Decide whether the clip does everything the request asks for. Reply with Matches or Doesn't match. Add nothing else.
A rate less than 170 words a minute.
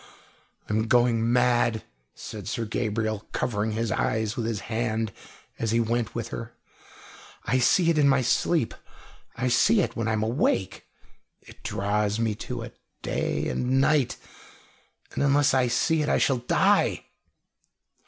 Matches